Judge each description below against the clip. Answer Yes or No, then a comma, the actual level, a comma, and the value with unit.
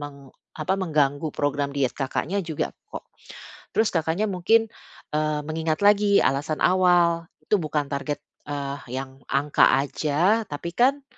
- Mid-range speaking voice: Yes, medium, 155 Hz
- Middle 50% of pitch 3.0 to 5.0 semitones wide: Yes, average, 4.6 semitones